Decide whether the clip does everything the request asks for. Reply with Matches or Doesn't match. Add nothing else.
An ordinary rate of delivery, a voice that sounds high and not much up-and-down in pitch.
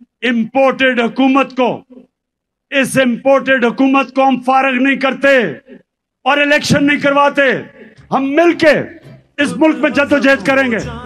Matches